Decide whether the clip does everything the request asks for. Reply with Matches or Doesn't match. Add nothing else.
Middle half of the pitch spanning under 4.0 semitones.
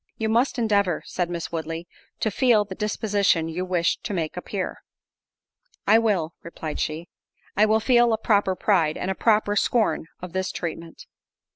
Doesn't match